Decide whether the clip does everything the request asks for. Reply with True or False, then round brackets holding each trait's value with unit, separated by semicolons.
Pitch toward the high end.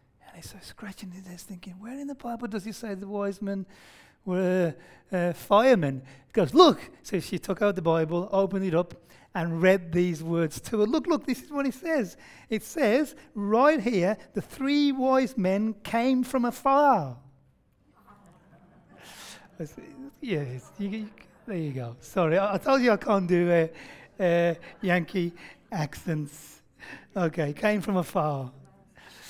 True (195 Hz)